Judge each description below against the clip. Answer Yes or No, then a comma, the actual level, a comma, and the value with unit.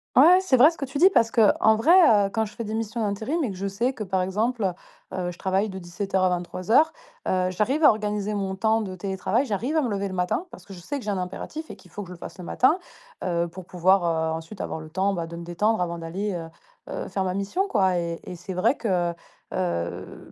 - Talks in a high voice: Yes, high, 195 Hz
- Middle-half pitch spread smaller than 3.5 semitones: No, average, 3.8 semitones